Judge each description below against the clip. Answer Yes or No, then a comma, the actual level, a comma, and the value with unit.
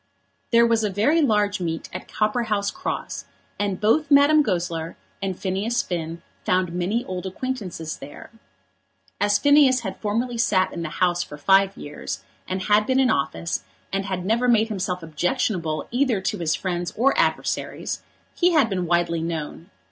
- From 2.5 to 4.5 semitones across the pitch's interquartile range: No, average, 5.0 semitones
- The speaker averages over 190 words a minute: No, average, 165 wpm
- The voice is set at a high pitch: Yes, high, 195 Hz